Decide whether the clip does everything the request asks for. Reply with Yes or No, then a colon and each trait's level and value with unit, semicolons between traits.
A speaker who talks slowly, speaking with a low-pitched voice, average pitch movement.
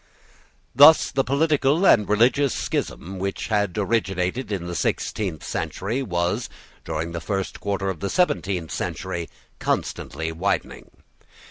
No: slow, 125 wpm; low, 100 Hz; wide, 5.8 semitones